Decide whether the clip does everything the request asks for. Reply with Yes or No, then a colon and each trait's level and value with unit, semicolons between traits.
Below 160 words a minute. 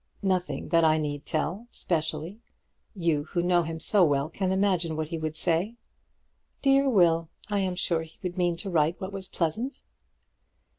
No: average, 170 wpm